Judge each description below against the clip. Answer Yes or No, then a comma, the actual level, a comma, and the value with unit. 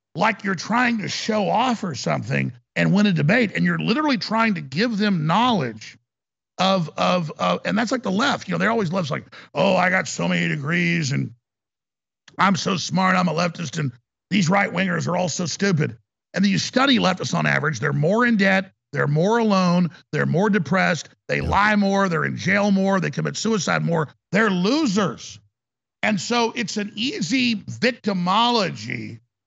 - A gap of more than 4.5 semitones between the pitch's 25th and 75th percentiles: Yes, average, 5.2 semitones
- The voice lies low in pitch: No, medium, 185 Hz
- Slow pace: No, average, 185 wpm